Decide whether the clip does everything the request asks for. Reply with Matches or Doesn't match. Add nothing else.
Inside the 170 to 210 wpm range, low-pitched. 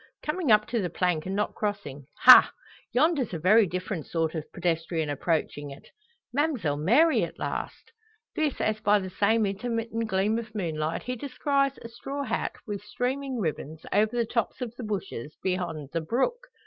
Doesn't match